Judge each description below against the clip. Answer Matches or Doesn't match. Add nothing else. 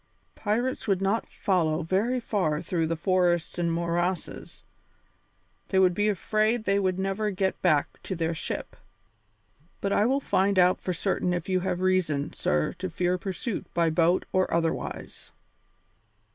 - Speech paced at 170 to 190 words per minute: Doesn't match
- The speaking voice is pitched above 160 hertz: Matches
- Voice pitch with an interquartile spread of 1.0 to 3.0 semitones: Matches